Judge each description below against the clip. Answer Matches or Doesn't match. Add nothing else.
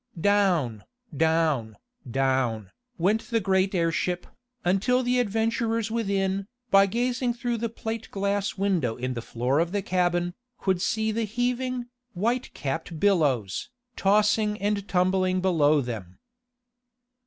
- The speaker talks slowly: Matches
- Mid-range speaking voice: Doesn't match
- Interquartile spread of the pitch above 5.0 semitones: Matches